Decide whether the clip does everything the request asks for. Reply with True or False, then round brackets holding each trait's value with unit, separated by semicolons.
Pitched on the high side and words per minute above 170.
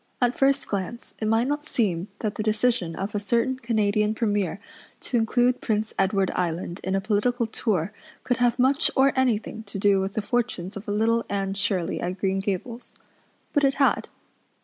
True (215 Hz; 180 wpm)